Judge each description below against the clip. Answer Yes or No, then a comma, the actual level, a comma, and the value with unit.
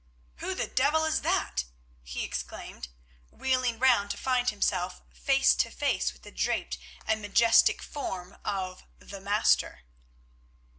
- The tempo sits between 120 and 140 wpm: Yes, slow, 135 wpm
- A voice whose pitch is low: No, high, 200 Hz